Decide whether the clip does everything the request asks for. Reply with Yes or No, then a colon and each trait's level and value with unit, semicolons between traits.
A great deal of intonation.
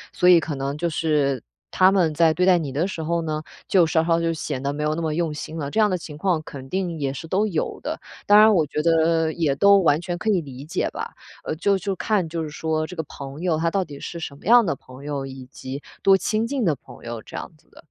No: average, 3.6 semitones